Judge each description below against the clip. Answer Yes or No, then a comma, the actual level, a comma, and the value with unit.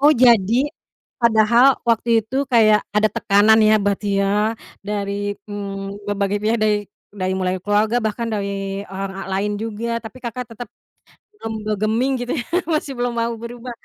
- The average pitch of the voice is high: Yes, high, 215 Hz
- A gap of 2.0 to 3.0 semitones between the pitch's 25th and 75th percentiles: Yes, narrow, 2.5 semitones